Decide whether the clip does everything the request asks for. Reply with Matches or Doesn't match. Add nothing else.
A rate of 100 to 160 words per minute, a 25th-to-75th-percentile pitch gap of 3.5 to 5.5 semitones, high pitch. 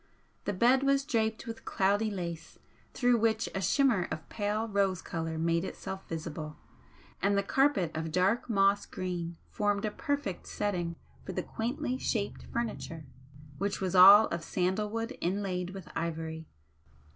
Matches